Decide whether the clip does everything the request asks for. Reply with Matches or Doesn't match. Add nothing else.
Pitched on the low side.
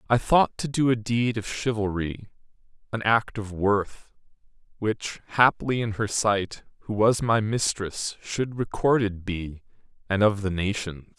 Matches